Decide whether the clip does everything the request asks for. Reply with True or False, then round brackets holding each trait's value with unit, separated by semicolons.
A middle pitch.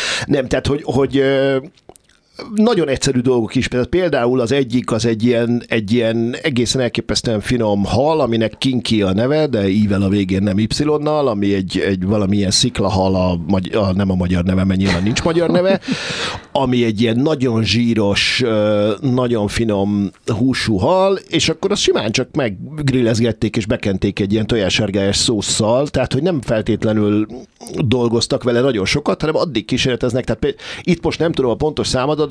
False (120 Hz)